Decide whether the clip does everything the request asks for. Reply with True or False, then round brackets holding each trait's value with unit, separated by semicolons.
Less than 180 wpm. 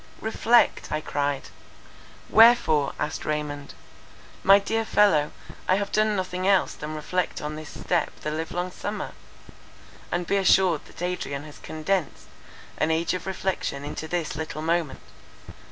True (140 wpm)